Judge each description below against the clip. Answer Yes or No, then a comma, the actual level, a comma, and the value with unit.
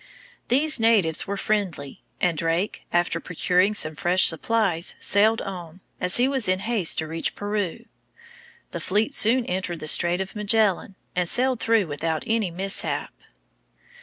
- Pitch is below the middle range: No, high, 190 Hz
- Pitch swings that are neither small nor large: Yes, average, 4.1 semitones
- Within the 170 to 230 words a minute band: No, average, 150 wpm